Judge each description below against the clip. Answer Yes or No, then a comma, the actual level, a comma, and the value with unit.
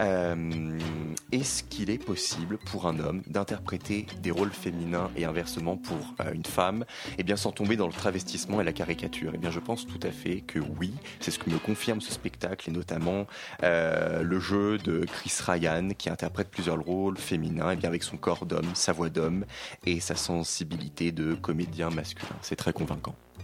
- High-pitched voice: No, very low, 85 Hz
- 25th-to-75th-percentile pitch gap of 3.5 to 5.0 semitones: No, average, 2.7 semitones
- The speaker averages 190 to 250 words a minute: Yes, average, 195 wpm